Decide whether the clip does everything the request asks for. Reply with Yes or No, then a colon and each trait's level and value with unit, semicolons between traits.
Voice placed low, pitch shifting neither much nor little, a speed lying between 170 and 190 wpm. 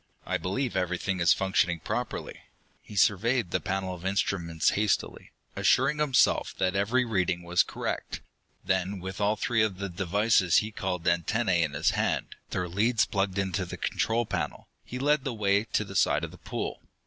Yes: very low, 95 Hz; average, 3.1 semitones; average, 175 wpm